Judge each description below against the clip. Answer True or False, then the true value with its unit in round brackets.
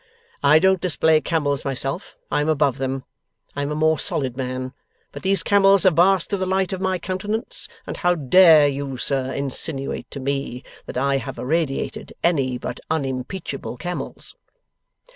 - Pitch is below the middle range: False (150 Hz)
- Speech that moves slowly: False (165 wpm)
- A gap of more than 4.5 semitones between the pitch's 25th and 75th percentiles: True (4.9 semitones)